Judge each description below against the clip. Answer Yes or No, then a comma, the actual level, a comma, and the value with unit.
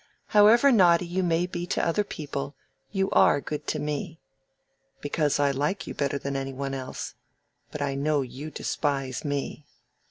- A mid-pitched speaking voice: Yes, medium, 150 Hz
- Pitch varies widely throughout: No, average, 3.8 semitones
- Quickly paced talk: No, average, 165 wpm